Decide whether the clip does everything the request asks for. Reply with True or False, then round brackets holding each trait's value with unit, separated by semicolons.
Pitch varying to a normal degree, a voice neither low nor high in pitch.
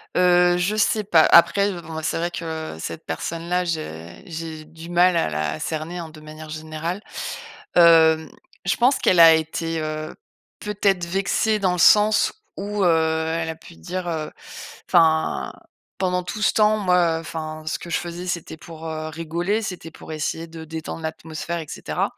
False (2.2 semitones; 165 Hz)